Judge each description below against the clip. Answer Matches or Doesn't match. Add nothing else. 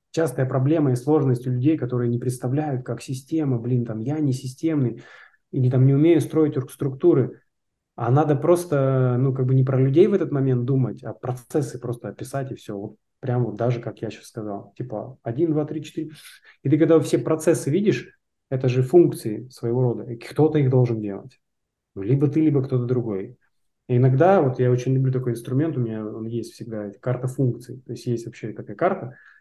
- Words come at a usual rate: Doesn't match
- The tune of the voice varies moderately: Matches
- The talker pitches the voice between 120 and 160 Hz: Matches